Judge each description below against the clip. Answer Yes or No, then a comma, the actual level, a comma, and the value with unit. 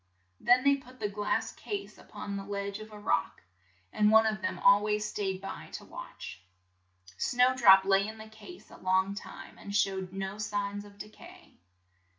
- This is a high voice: Yes, high, 205 Hz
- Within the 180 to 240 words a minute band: Yes, average, 195 wpm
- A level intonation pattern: Yes, narrow, 1.8 semitones